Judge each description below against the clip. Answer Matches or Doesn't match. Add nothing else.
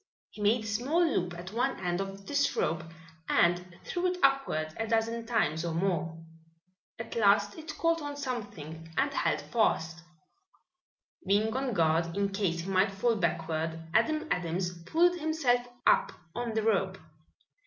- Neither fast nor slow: Matches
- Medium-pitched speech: Doesn't match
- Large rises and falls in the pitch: Matches